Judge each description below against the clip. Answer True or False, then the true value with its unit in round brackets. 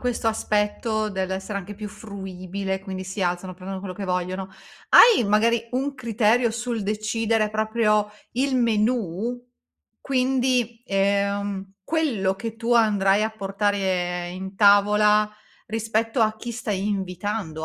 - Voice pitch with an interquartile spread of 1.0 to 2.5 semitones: False (2.9 semitones)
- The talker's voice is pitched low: False (210 Hz)